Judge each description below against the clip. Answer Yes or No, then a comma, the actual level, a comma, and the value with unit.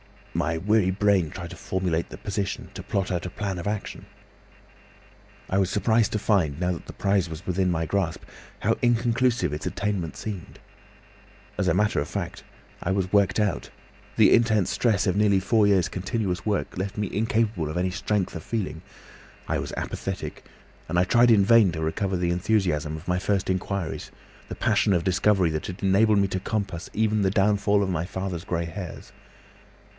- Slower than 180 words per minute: No, average, 185 wpm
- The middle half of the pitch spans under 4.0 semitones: Yes, average, 2.9 semitones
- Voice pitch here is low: Yes, very low, 95 Hz